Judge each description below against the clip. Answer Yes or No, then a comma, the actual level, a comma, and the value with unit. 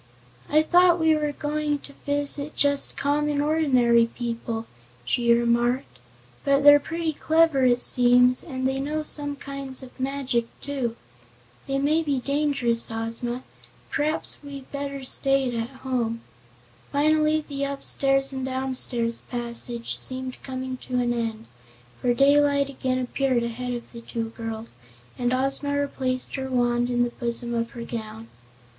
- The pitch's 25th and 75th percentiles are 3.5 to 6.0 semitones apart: No, average, 3.0 semitones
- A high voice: Yes, very high, 260 Hz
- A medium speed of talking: Yes, average, 145 wpm